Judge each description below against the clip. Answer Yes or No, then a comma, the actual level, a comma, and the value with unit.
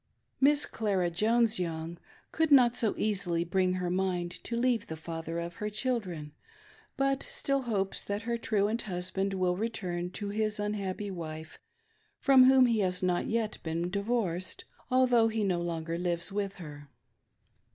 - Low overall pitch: No, high, 195 Hz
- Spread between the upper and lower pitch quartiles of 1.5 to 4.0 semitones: No, average, 4.7 semitones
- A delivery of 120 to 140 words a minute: No, average, 155 wpm